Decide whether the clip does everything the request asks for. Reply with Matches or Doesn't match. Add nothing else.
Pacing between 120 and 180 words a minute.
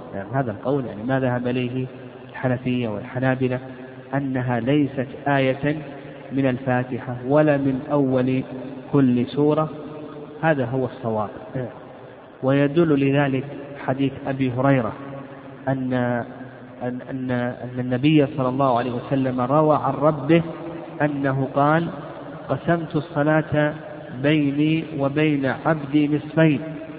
Doesn't match